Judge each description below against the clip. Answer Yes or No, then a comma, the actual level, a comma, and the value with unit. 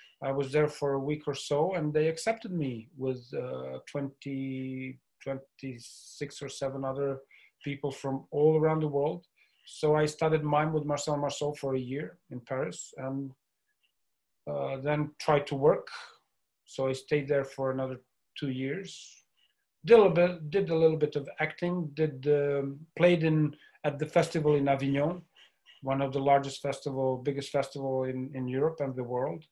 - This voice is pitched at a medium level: Yes, medium, 145 Hz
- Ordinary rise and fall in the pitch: No, narrow, 2.2 semitones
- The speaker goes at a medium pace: Yes, average, 170 wpm